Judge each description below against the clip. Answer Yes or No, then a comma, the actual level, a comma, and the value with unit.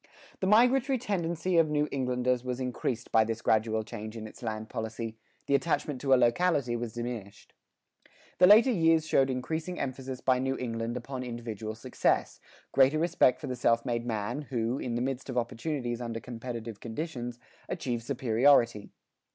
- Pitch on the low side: Yes, low, 125 Hz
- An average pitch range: Yes, average, 3.7 semitones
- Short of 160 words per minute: No, average, 165 wpm